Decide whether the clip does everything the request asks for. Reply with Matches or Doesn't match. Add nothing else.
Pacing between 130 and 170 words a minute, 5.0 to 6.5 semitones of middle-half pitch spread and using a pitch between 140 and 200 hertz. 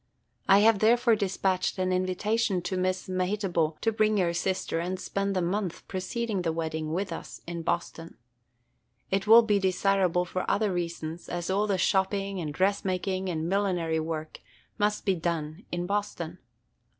Doesn't match